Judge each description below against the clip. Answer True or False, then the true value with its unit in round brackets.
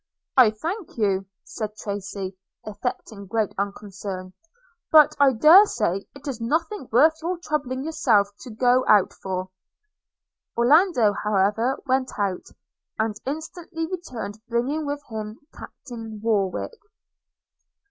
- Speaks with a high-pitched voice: True (230 Hz)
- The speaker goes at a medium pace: False (115 wpm)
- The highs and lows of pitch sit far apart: True (6.4 semitones)